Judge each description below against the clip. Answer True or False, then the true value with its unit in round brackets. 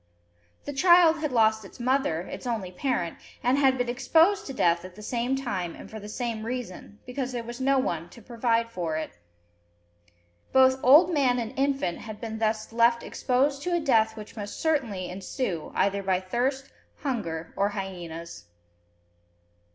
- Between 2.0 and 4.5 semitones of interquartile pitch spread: False (5.2 semitones)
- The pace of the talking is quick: False (170 wpm)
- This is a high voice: True (235 Hz)